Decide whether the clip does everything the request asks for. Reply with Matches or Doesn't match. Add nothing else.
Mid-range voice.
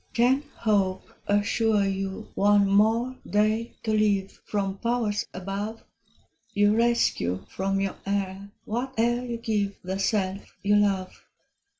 Doesn't match